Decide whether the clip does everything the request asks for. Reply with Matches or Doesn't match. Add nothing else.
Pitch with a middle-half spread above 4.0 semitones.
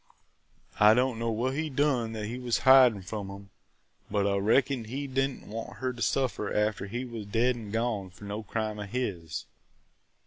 Doesn't match